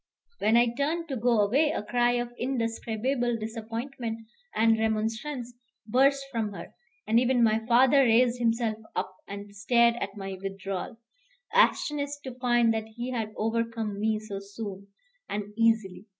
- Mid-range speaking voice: No, high, 230 Hz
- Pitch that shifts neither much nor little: No, narrow, 2.3 semitones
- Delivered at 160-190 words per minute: No, average, 150 wpm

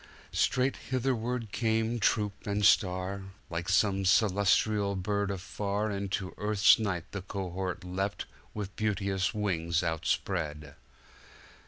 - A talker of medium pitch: No, low, 100 Hz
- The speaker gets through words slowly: Yes, slow, 105 wpm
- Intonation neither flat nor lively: No, narrow, 2.3 semitones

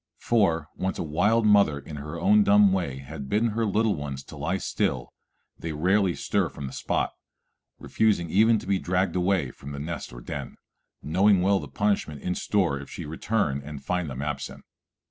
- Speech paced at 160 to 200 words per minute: Yes, average, 185 wpm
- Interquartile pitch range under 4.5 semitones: No, wide, 5.6 semitones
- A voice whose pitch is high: No, very low, 90 Hz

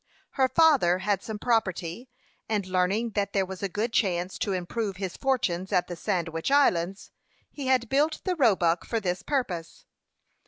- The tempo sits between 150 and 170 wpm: Yes, average, 165 wpm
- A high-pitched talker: Yes, high, 200 Hz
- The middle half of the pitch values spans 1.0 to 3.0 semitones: No, average, 5.2 semitones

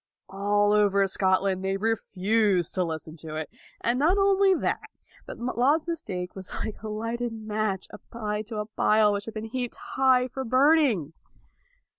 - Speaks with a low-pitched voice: No, high, 215 Hz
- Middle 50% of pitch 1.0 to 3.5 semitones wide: No, average, 4.4 semitones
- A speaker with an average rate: Yes, average, 160 wpm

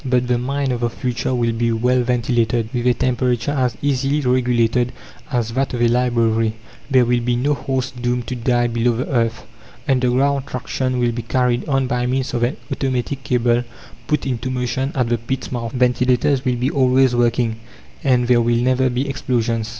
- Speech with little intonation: Yes, narrow, 1.4 semitones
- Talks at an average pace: Yes, average, 190 wpm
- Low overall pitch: Yes, low, 125 Hz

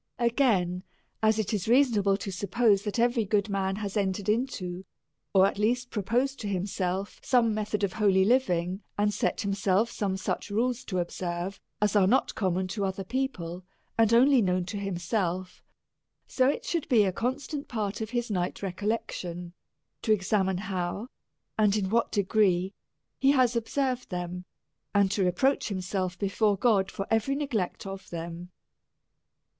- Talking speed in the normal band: Yes, average, 160 wpm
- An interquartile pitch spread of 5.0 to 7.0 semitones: No, average, 3.7 semitones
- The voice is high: Yes, high, 200 Hz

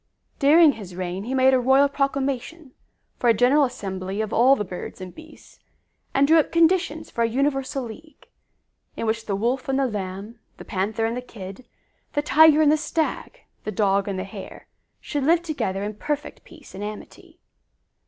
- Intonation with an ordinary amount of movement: No, wide, 6.0 semitones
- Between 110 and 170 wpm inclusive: No, average, 185 wpm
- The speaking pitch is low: No, very high, 250 Hz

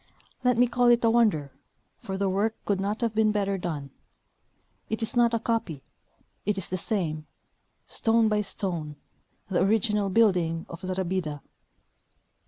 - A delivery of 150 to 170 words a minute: Yes, average, 160 wpm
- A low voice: No, high, 200 Hz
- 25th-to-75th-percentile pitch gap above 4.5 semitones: No, average, 4.1 semitones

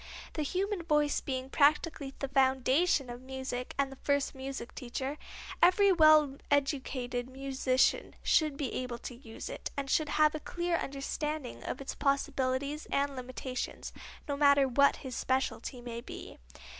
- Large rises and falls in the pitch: No, narrow, 2.5 semitones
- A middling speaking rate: Yes, average, 150 wpm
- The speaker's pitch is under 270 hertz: No, very high, 275 Hz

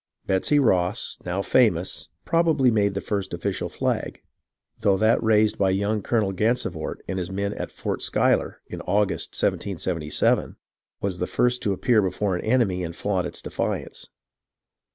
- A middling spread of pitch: Yes, average, 3.0 semitones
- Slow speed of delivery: No, average, 155 wpm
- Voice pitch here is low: Yes, low, 100 Hz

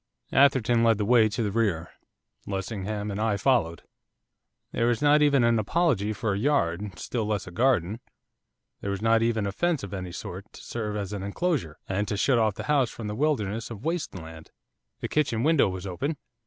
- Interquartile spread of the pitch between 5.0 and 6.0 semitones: No, average, 4.0 semitones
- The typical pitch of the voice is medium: No, low, 110 Hz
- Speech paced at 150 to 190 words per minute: No, average, 200 wpm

